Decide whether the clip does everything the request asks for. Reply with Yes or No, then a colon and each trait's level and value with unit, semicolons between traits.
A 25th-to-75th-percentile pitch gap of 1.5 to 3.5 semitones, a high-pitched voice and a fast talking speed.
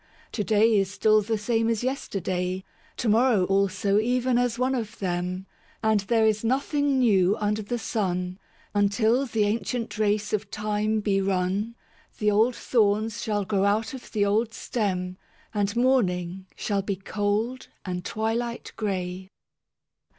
No: average, 2.8 semitones; high, 210 Hz; average, 150 wpm